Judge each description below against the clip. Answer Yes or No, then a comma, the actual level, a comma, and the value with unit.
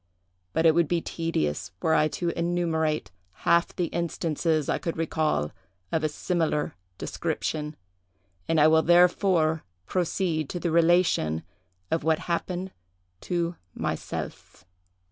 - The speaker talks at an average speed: No, slow, 125 wpm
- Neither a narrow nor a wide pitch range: No, narrow, 1.9 semitones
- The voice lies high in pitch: No, medium, 165 Hz